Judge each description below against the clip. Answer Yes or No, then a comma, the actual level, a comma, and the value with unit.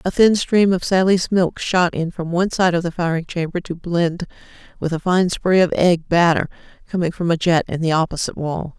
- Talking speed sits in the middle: No, fast, 220 wpm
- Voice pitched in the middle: Yes, medium, 175 Hz